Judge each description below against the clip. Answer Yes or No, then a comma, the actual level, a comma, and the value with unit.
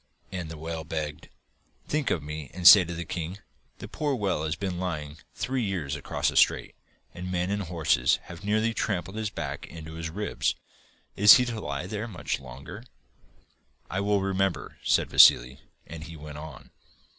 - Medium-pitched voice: No, very low, 90 Hz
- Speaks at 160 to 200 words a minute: Yes, average, 180 wpm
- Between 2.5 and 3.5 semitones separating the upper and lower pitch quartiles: No, average, 4.5 semitones